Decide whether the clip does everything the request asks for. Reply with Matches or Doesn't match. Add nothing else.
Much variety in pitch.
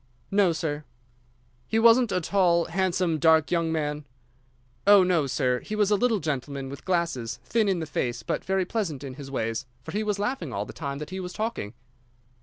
Matches